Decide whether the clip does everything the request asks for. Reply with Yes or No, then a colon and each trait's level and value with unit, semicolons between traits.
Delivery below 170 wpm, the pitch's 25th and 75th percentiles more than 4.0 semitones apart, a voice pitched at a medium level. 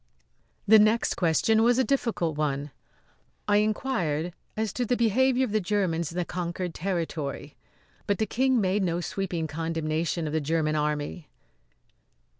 Yes: average, 150 wpm; wide, 5.4 semitones; medium, 180 Hz